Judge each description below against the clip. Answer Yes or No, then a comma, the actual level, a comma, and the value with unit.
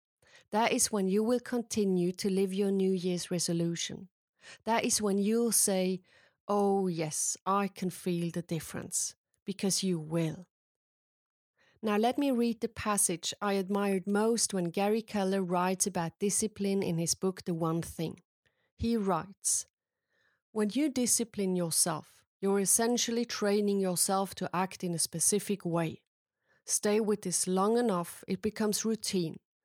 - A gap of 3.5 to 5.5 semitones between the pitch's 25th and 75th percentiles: No, average, 3.0 semitones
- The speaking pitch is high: Yes, high, 195 Hz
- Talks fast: No, average, 145 wpm